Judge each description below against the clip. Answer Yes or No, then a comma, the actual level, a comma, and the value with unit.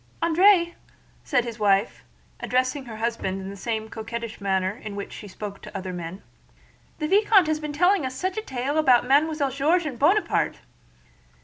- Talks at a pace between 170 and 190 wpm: Yes, average, 175 wpm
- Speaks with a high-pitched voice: Yes, very high, 255 Hz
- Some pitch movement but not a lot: No, wide, 6.8 semitones